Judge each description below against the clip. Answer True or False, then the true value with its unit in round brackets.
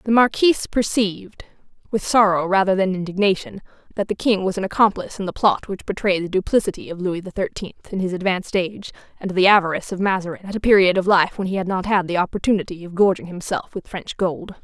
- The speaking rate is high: True (215 wpm)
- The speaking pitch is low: False (190 Hz)